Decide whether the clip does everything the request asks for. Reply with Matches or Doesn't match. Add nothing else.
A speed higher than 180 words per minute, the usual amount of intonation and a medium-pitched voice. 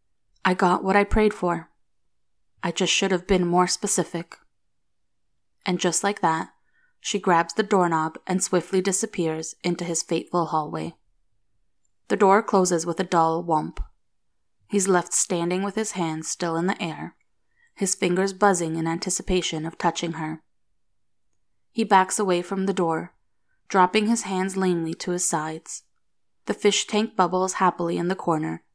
Doesn't match